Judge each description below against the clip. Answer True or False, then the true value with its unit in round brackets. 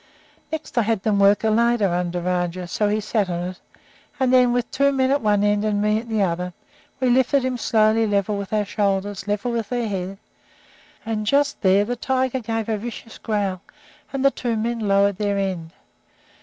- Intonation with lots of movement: False (3.3 semitones)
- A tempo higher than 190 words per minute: True (205 wpm)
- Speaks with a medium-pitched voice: False (215 Hz)